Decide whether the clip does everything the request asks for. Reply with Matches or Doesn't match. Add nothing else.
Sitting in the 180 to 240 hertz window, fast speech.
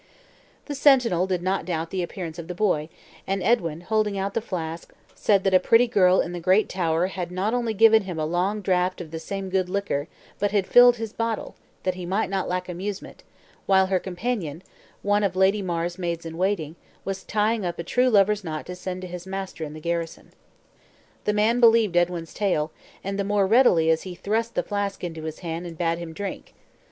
Matches